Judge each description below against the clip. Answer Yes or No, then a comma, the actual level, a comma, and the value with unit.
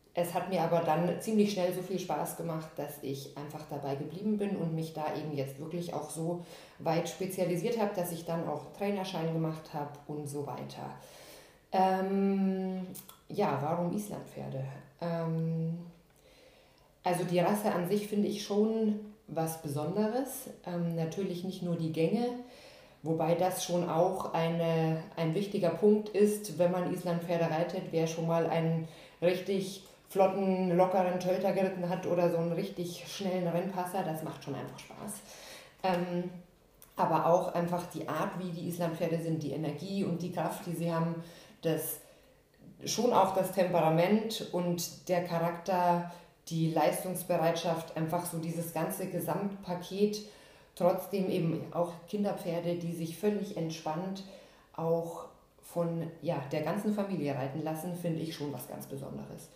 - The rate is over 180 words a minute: No, average, 150 wpm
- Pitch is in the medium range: Yes, medium, 175 Hz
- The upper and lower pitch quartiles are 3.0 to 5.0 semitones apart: No, narrow, 2.5 semitones